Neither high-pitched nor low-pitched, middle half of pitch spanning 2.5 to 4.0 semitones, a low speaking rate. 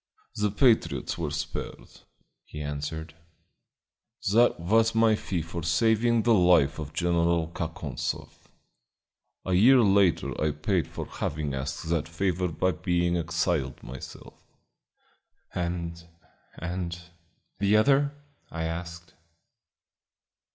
No: very low, 85 Hz; average, 3.7 semitones; slow, 110 wpm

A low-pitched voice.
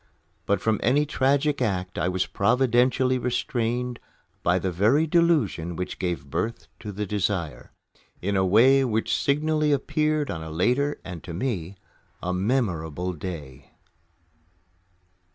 Yes: low, 110 Hz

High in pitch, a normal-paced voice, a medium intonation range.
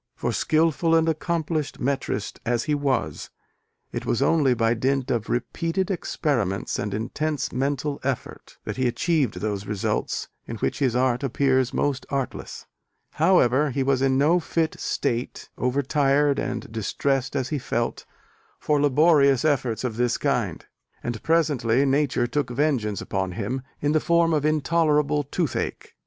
No: low, 135 Hz; average, 150 wpm; average, 3.8 semitones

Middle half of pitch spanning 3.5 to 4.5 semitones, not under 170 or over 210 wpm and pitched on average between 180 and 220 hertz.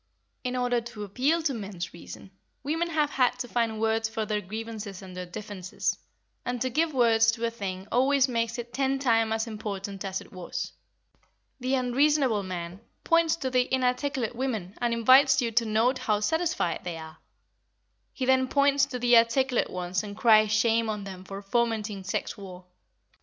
No: average, 4.0 semitones; average, 180 wpm; high, 230 Hz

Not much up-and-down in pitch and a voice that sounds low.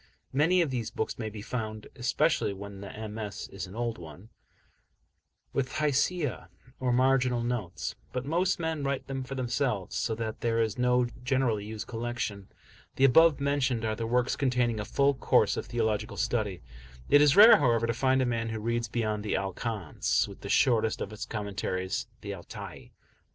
No: average, 3.5 semitones; low, 120 Hz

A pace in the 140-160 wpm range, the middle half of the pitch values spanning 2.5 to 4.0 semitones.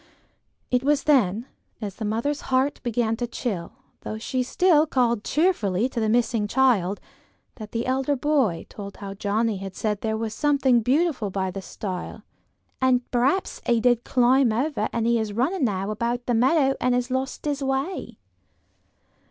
No: average, 170 wpm; average, 3.7 semitones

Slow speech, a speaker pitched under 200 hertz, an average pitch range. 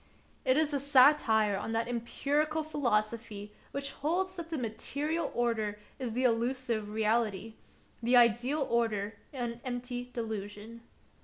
No: slow, 130 wpm; high, 240 Hz; average, 4.1 semitones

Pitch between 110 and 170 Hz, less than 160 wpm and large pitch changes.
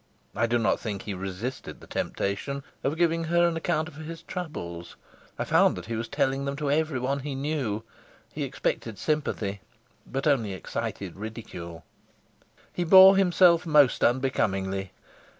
Yes: low, 135 Hz; average, 150 wpm; wide, 7.3 semitones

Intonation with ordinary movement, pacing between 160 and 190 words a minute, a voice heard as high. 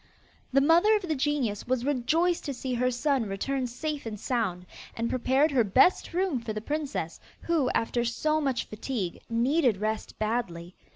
Yes: average, 4.5 semitones; average, 170 wpm; very high, 255 Hz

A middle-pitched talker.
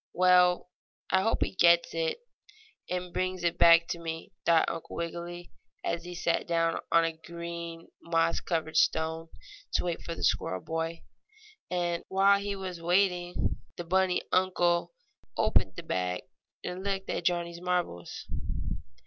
Yes: medium, 170 Hz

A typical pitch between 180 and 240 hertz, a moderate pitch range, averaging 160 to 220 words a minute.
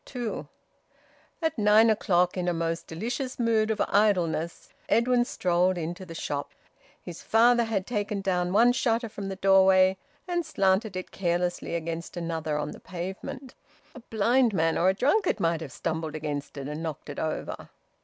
Yes: high, 190 Hz; average, 5.0 semitones; average, 165 wpm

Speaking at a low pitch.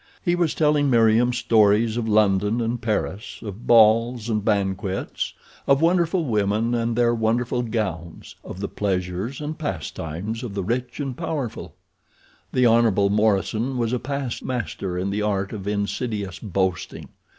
Yes: low, 110 Hz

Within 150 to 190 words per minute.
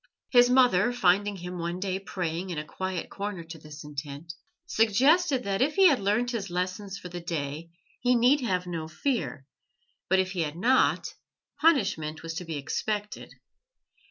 Yes: average, 170 wpm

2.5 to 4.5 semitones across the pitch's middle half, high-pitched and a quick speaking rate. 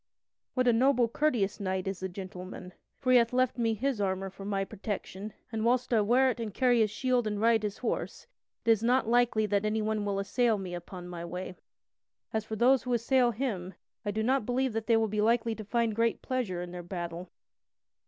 Yes: average, 3.7 semitones; high, 220 Hz; fast, 215 wpm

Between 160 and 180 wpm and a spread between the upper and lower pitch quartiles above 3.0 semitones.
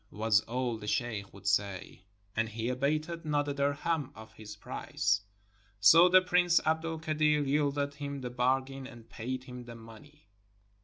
Yes: average, 165 wpm; average, 5.1 semitones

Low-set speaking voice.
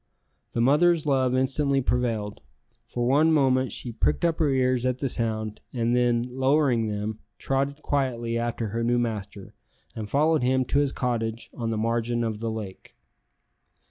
Yes: low, 125 Hz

